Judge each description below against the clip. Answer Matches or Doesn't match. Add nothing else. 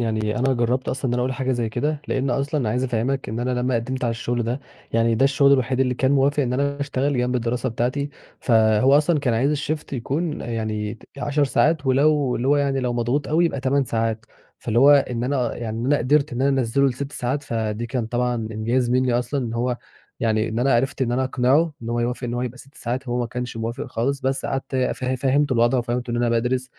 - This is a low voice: Matches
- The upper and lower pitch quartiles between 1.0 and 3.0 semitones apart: Matches